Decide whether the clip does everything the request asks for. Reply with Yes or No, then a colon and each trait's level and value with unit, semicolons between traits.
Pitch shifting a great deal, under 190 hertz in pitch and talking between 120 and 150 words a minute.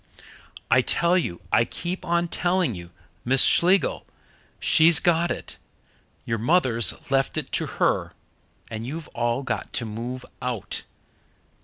Yes: wide, 6.6 semitones; low, 135 Hz; slow, 135 wpm